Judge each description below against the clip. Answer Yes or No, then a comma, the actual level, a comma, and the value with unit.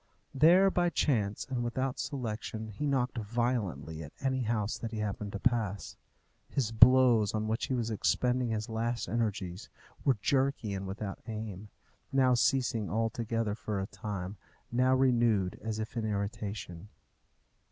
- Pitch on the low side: Yes, low, 115 Hz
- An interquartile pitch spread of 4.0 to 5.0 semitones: No, average, 3.3 semitones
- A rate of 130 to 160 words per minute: Yes, average, 150 wpm